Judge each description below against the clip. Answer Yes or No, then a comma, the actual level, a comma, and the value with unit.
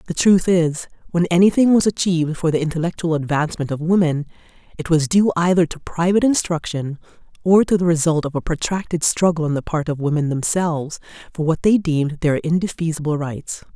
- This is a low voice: No, medium, 165 Hz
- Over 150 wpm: Yes, average, 180 wpm